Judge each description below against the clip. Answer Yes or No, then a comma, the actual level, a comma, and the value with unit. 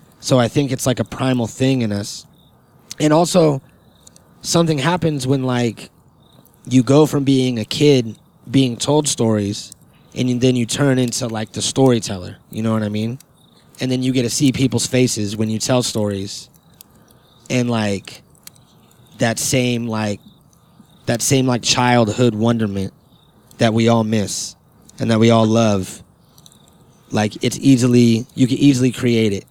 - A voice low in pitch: Yes, low, 120 Hz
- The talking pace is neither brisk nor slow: Yes, average, 155 wpm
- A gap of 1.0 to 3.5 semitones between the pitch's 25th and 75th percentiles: Yes, average, 3.1 semitones